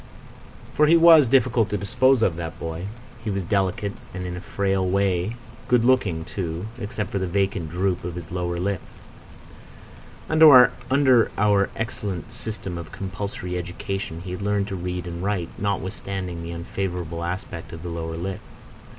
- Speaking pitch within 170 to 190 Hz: No, very low, 95 Hz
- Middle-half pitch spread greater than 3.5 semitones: No, average, 3.0 semitones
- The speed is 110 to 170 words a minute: Yes, average, 160 wpm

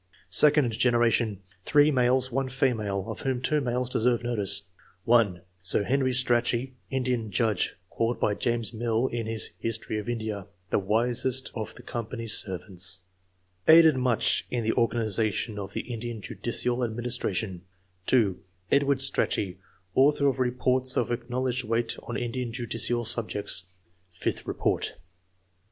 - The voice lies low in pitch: Yes, low, 120 Hz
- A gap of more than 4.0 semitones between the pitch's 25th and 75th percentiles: No, average, 3.0 semitones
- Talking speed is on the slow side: No, average, 145 wpm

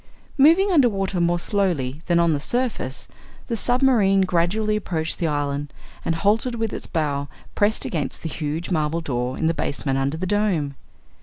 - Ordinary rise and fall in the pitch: No, wide, 6.0 semitones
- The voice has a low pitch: No, medium, 170 Hz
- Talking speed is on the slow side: No, average, 170 wpm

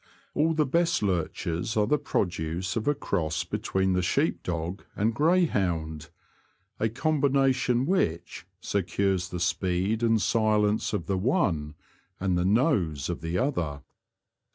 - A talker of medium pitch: No, low, 100 Hz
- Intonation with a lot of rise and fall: Yes, wide, 6.7 semitones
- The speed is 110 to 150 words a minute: Yes, average, 145 wpm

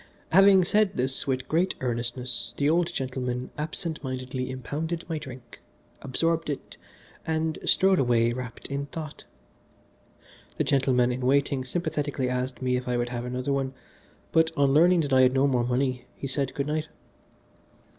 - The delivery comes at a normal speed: Yes, average, 160 wpm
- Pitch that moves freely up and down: No, average, 3.7 semitones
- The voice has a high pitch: No, low, 135 Hz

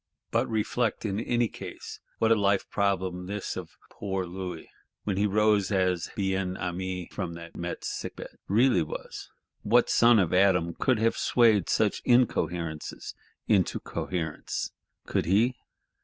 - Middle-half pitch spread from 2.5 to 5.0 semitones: Yes, average, 3.2 semitones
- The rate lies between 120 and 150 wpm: Yes, average, 145 wpm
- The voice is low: Yes, very low, 95 Hz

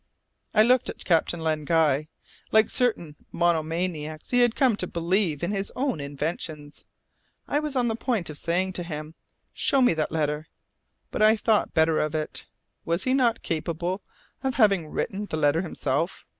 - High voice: No, medium, 170 Hz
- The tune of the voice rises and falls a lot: Yes, wide, 5.8 semitones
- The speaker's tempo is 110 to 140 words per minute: No, average, 170 wpm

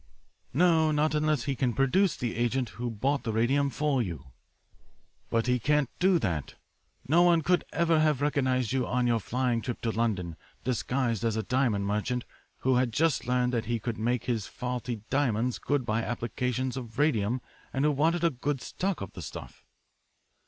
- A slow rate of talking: No, average, 180 wpm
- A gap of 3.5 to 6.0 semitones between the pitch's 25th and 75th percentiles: Yes, average, 4.0 semitones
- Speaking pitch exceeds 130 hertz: No, low, 125 Hz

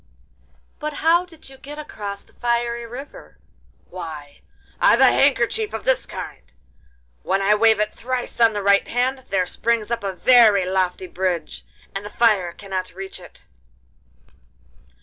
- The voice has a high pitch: Yes, high, 210 Hz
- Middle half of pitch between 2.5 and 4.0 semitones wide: No, average, 4.8 semitones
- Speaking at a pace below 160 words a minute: Yes, average, 150 wpm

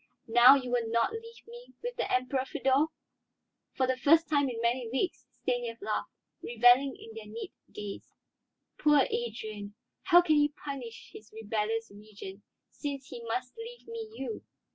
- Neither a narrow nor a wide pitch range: Yes, average, 4.6 semitones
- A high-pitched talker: Yes, very high, 255 Hz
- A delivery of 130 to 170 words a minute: Yes, average, 160 wpm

